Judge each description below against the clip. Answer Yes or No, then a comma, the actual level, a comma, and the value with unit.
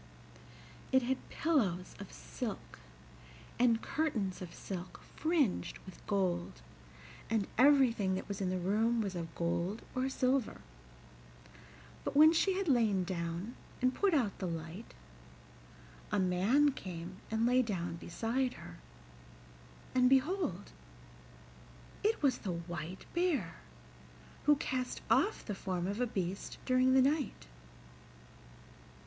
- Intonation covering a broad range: Yes, wide, 6.5 semitones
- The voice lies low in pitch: No, high, 215 Hz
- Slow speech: Yes, slow, 125 wpm